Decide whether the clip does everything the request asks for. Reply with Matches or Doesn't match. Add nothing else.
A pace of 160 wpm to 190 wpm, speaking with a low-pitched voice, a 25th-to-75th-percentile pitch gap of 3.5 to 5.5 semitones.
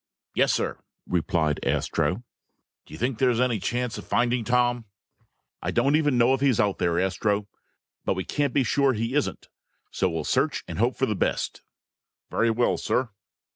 Matches